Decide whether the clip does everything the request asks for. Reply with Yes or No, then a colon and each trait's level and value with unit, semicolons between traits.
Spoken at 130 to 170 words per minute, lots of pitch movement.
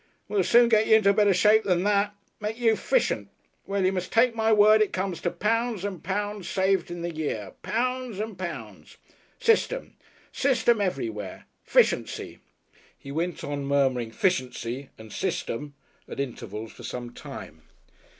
Yes: average, 155 wpm; wide, 7.3 semitones